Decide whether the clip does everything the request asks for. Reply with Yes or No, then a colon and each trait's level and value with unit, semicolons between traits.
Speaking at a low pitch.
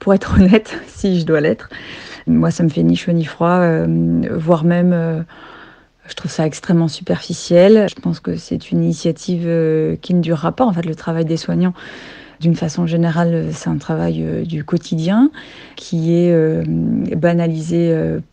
No: medium, 165 Hz